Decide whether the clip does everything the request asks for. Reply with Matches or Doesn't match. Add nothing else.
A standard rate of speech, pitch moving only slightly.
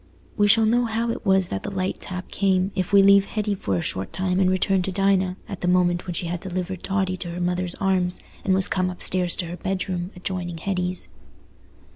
Doesn't match